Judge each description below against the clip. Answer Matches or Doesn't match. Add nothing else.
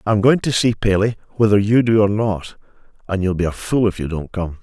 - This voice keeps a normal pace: Doesn't match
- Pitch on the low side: Matches